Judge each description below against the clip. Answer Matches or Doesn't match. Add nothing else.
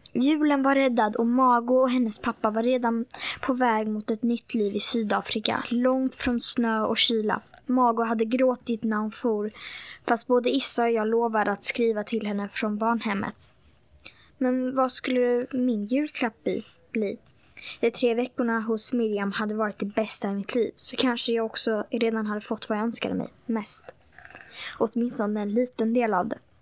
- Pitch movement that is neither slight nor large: Doesn't match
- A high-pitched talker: Matches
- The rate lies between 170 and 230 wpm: Matches